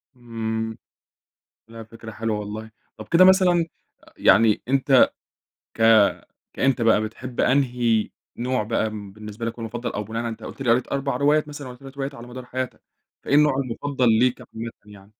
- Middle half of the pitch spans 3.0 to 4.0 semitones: Yes, average, 3.3 semitones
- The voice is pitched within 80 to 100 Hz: No, low, 120 Hz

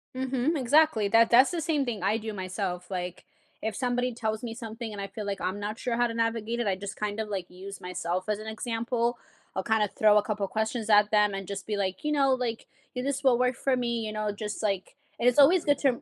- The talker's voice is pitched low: No, high, 220 Hz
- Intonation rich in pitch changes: No, average, 3.4 semitones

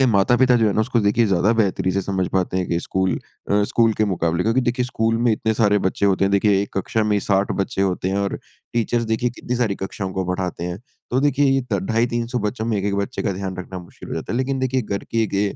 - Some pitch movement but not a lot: Yes, average, 3.6 semitones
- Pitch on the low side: Yes, low, 105 Hz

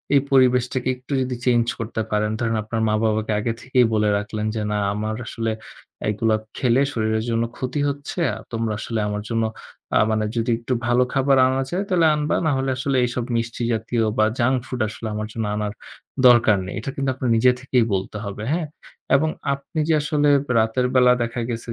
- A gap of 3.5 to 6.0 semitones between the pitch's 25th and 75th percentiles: No, average, 3.0 semitones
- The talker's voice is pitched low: Yes, low, 120 Hz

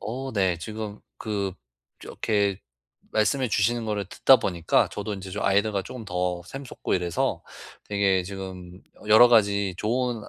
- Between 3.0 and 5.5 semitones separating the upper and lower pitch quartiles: No, narrow, 2.6 semitones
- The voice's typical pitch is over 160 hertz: No, low, 100 Hz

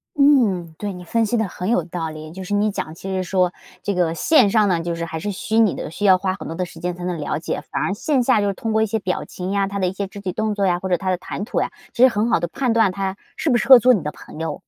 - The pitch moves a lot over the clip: No, average, 3.4 semitones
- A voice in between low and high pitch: No, high, 195 Hz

